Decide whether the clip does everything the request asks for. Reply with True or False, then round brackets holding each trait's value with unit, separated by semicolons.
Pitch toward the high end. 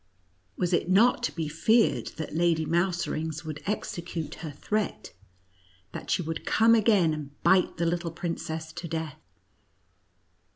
False (170 Hz)